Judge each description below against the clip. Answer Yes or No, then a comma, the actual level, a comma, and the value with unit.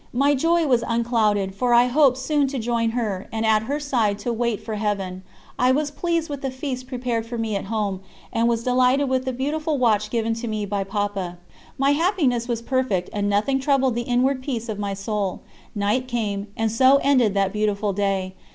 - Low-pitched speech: No, high, 235 Hz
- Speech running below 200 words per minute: No, fast, 205 wpm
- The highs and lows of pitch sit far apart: No, average, 4.0 semitones